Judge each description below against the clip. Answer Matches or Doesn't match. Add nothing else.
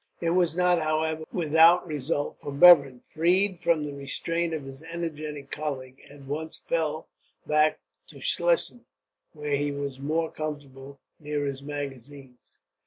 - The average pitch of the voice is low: Doesn't match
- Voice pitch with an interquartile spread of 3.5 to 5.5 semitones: Doesn't match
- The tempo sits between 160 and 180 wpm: Doesn't match